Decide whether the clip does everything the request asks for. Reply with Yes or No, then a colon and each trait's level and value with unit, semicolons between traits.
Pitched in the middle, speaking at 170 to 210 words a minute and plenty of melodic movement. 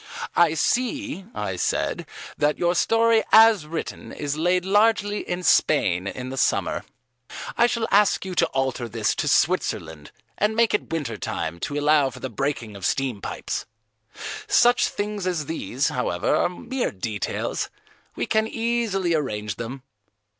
No: medium, 160 Hz; average, 155 wpm; wide, 9.0 semitones